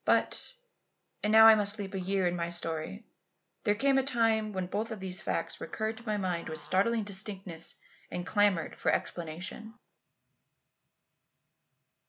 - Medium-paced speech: Yes, average, 155 wpm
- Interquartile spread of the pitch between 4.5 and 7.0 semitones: No, average, 3.5 semitones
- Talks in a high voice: Yes, high, 200 Hz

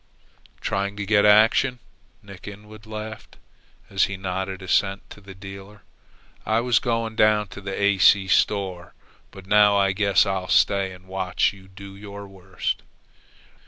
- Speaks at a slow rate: No, average, 155 wpm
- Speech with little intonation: Yes, narrow, 1.6 semitones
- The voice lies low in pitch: Yes, low, 100 Hz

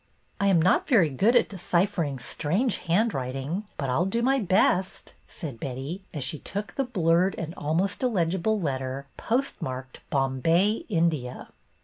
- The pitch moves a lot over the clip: Yes, wide, 6.6 semitones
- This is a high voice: No, medium, 170 Hz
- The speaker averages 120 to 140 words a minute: No, average, 150 wpm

